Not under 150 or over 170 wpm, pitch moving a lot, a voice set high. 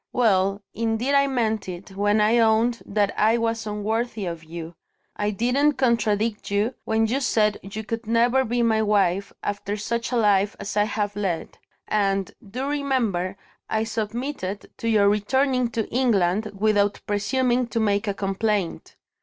No: average, 160 wpm; narrow, 2.6 semitones; high, 215 Hz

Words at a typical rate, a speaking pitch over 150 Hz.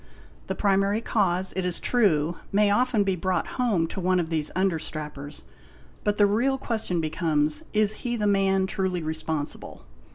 Yes: average, 160 wpm; high, 190 Hz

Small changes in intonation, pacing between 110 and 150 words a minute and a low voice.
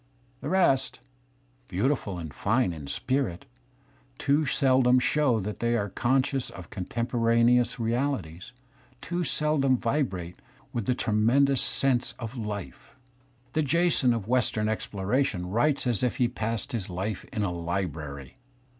No: average, 5.1 semitones; average, 145 wpm; low, 120 Hz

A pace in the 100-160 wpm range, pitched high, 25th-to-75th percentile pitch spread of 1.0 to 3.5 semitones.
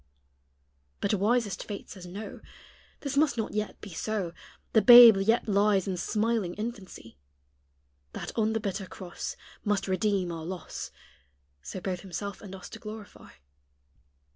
Yes: average, 140 wpm; high, 200 Hz; average, 2.8 semitones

